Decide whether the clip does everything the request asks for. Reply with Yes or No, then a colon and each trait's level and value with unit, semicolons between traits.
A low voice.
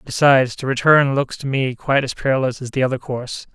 Yes: low, 130 Hz